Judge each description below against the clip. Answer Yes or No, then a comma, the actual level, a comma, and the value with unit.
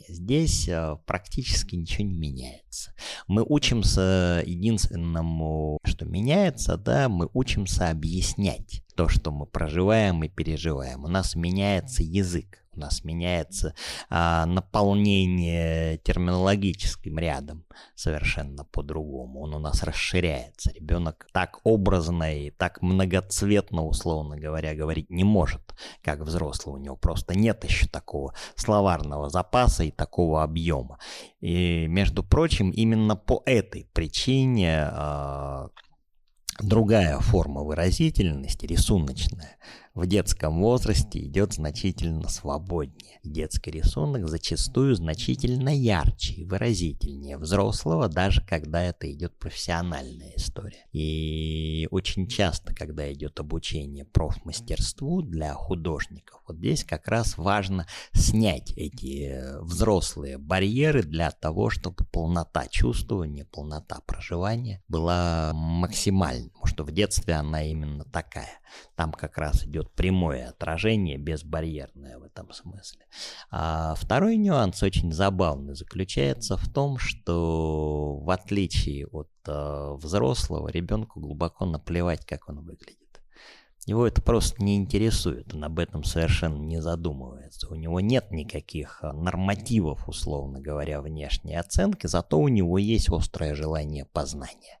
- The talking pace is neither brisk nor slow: Yes, average, 120 wpm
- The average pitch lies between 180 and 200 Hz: No, very low, 85 Hz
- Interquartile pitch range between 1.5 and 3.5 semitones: No, average, 4.1 semitones